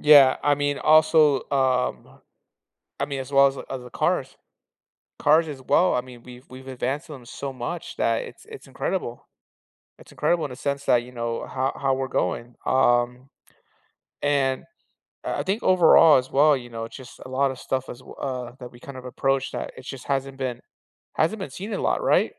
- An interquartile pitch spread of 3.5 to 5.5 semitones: No, narrow, 2.4 semitones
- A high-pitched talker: No, low, 135 Hz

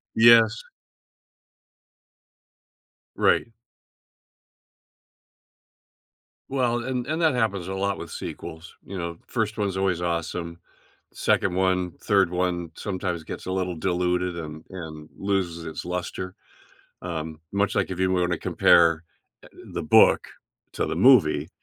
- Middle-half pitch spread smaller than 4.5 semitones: Yes, average, 2.9 semitones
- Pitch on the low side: Yes, very low, 90 Hz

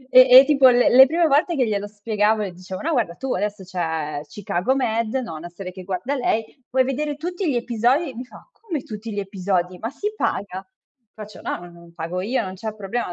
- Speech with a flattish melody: No, wide, 5.9 semitones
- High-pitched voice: Yes, high, 220 Hz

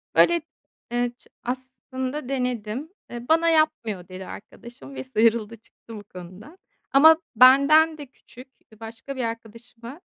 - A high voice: Yes, high, 245 Hz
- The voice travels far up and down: No, average, 3.9 semitones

